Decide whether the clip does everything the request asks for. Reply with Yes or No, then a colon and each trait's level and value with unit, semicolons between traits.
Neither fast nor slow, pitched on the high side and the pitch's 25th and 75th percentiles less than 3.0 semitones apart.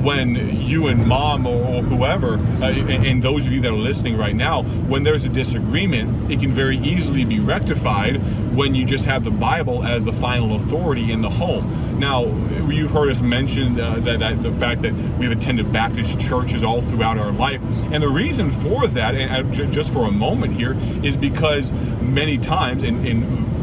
No: average, 195 wpm; low, 120 Hz; narrow, 2.5 semitones